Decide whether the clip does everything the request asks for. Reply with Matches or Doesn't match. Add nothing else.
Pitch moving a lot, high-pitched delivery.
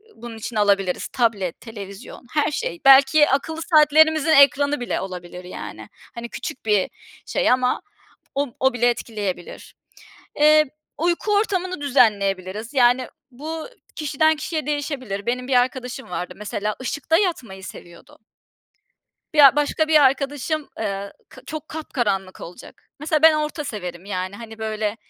Matches